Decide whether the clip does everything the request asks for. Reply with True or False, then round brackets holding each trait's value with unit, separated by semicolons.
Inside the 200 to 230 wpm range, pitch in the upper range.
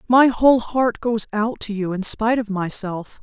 True (205 wpm; 220 Hz)